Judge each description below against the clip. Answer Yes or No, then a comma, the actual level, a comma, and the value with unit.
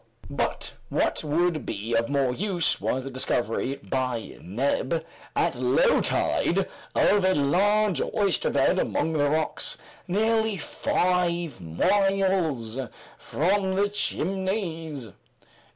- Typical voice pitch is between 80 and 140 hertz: No, medium, 165 Hz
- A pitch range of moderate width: No, wide, 6.4 semitones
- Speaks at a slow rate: Yes, slow, 105 wpm